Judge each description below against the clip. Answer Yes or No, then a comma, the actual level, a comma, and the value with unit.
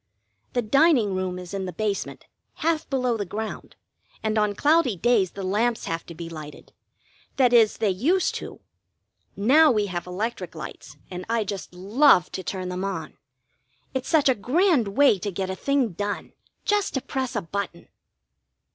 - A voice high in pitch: Yes, high, 210 Hz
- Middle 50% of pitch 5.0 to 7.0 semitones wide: Yes, wide, 5.6 semitones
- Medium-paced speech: Yes, average, 175 wpm